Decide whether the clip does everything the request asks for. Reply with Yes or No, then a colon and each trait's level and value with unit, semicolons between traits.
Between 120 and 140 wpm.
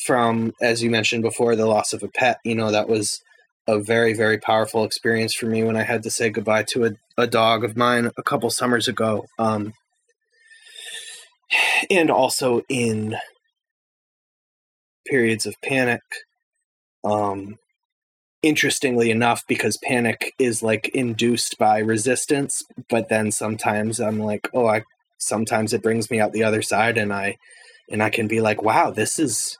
No: average, 160 wpm